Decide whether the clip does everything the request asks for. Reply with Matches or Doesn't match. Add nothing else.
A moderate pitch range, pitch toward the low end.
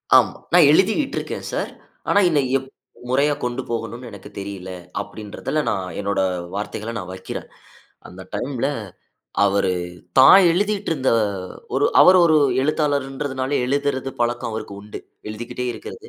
Doesn't match